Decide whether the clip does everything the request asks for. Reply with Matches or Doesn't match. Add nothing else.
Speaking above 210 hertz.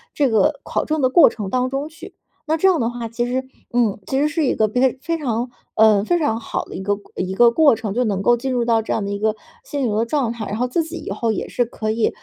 Matches